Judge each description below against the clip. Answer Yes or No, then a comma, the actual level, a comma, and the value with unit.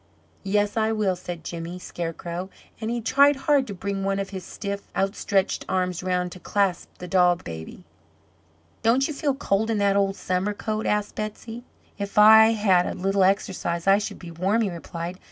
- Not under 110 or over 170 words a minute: No, average, 185 wpm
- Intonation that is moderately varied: Yes, average, 3.0 semitones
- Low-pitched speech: No, high, 195 Hz